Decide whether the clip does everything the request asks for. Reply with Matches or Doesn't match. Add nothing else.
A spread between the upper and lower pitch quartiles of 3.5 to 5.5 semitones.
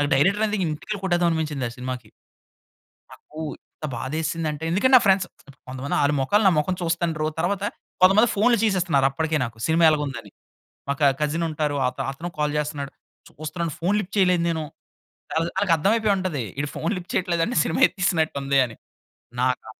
Matches